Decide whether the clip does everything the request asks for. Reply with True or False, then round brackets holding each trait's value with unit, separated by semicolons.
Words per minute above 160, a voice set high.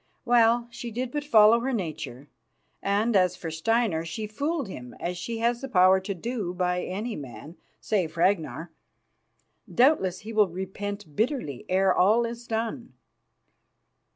False (150 wpm; 205 Hz)